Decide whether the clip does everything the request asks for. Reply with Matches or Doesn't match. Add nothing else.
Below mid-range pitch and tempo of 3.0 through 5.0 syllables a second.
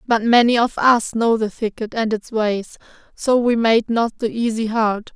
Doesn't match